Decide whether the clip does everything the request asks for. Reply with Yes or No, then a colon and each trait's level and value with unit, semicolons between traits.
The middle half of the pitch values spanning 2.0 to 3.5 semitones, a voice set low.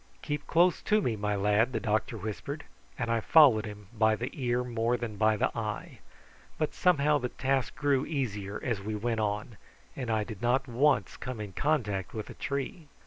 No: average, 4.4 semitones; low, 115 Hz